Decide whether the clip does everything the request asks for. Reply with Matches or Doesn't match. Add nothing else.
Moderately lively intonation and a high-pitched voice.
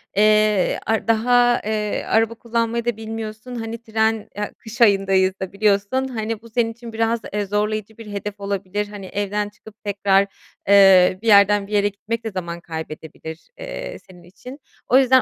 Doesn't match